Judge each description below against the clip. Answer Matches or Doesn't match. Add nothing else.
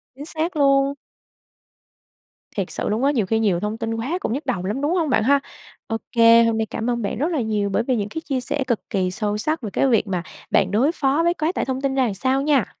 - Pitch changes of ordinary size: Matches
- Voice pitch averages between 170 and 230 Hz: Doesn't match